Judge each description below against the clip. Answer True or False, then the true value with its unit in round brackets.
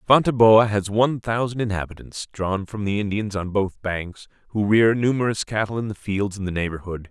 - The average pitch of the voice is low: True (105 Hz)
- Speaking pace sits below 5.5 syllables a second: True (5.3 syllables/s)